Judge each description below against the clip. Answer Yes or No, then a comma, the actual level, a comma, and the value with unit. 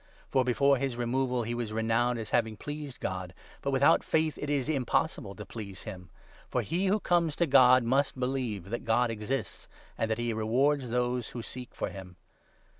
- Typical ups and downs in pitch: Yes, average, 3.6 semitones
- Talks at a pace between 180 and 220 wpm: Yes, average, 190 wpm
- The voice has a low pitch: Yes, low, 125 Hz